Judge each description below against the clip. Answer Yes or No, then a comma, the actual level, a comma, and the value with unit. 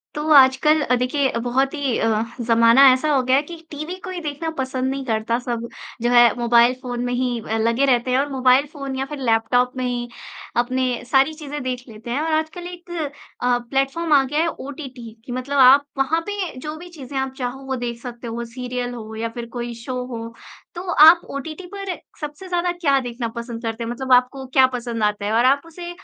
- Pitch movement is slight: No, average, 3.4 semitones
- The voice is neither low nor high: No, very high, 260 Hz